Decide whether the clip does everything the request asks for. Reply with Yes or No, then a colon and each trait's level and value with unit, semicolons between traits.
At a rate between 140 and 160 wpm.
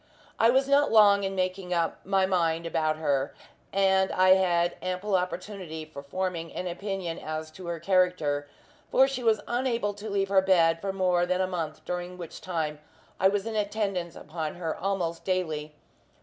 No: average, 175 wpm